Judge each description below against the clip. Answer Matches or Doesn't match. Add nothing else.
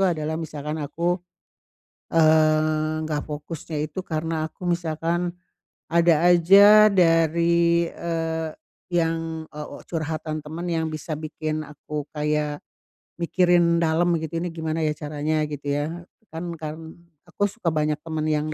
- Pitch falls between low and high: Matches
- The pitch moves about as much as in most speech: Doesn't match